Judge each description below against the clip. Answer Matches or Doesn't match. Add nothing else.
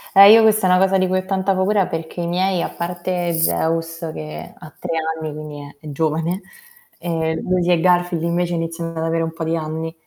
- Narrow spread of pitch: Matches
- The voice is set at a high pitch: Doesn't match